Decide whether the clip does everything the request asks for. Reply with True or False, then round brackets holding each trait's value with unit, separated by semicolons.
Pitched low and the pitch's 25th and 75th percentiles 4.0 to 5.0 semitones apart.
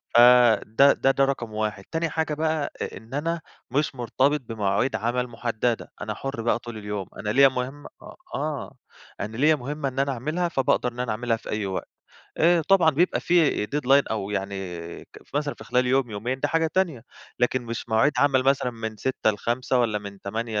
True (125 Hz; 4.4 semitones)